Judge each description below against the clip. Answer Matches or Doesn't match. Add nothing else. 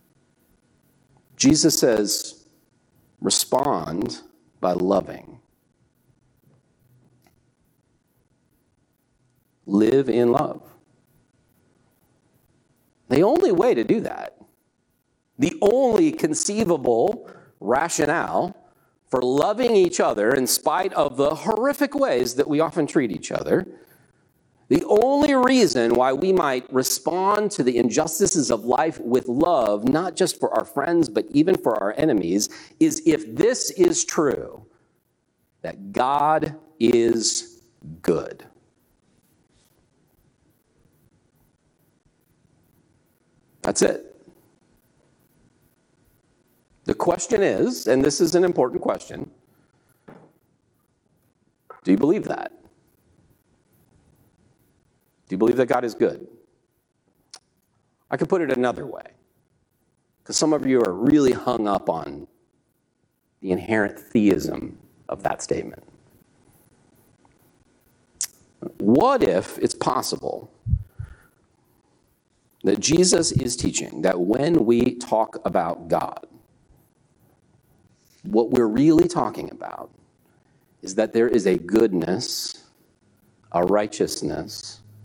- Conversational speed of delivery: Doesn't match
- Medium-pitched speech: Matches